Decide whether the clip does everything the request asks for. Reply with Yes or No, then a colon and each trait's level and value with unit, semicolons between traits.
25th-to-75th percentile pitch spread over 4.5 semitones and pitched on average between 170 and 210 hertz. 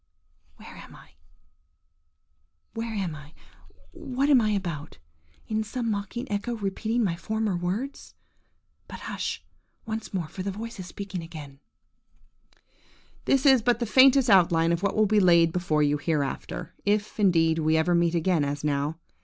Yes: wide, 5.4 semitones; medium, 185 Hz